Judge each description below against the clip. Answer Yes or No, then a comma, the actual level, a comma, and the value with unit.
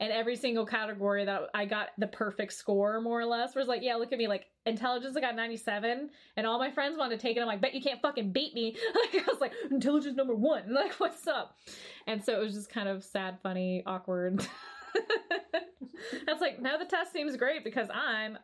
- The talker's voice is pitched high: Yes, high, 235 Hz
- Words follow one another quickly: Yes, fast, 225 wpm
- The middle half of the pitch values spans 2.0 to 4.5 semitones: No, average, 4.9 semitones